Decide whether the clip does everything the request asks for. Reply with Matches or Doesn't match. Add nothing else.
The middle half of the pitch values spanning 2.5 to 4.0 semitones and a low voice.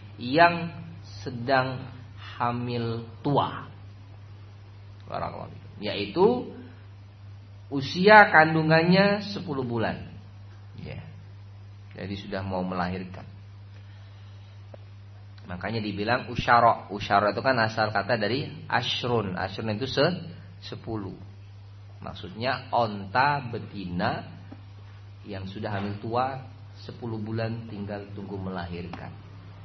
Matches